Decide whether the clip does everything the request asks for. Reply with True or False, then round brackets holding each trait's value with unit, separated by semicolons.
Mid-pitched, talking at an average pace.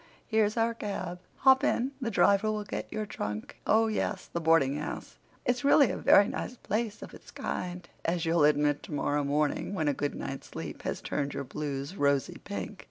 True (180 Hz; 175 wpm)